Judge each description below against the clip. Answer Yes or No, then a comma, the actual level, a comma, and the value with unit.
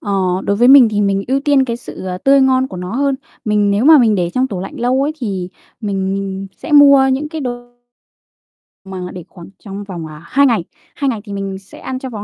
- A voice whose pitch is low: No, high, 215 Hz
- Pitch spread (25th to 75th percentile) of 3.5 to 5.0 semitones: No, wide, 5.4 semitones